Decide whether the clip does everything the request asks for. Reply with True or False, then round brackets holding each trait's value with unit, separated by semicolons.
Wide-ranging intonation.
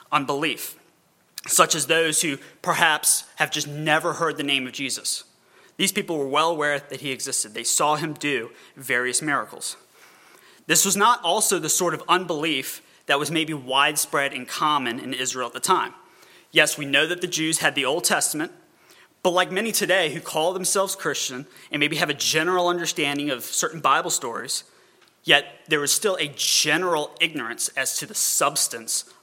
False (4.3 semitones)